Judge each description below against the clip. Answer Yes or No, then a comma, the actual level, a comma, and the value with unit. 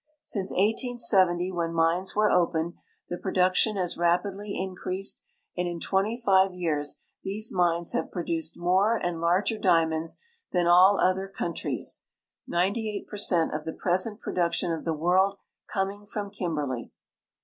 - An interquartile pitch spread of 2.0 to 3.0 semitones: Yes, average, 2.7 semitones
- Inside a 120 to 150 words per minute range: Yes, average, 140 wpm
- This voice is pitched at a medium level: Yes, medium, 180 Hz